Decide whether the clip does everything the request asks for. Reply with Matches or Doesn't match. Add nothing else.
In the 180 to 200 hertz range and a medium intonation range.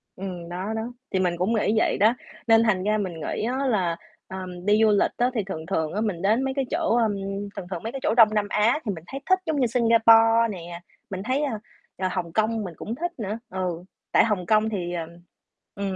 Doesn't match